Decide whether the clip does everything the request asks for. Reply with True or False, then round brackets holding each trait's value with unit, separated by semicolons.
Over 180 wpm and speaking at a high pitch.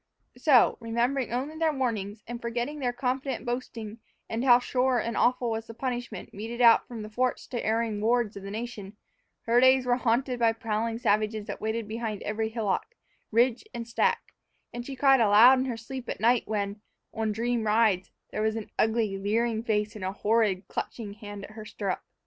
True (195 wpm; 230 Hz)